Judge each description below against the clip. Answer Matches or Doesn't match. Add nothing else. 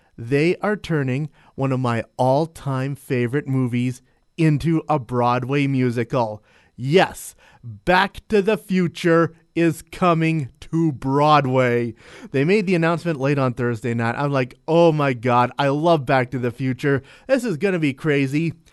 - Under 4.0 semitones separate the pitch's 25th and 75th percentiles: Doesn't match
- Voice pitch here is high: Doesn't match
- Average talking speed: Matches